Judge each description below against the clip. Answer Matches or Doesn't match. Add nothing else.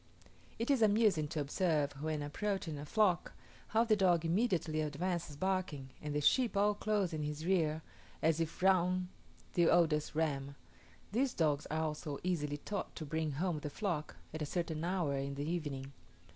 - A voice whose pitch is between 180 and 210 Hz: Doesn't match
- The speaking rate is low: Doesn't match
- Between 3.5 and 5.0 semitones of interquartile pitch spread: Matches